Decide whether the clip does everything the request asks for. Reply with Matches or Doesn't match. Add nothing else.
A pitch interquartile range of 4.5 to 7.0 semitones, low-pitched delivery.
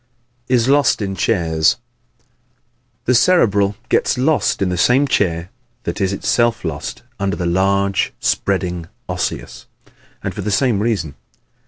Matches